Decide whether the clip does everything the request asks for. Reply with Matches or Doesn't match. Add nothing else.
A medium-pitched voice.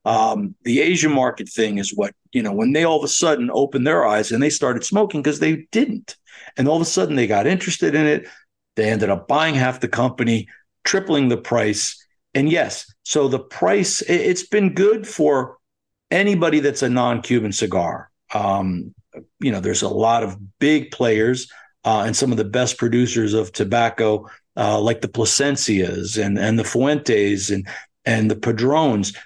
Doesn't match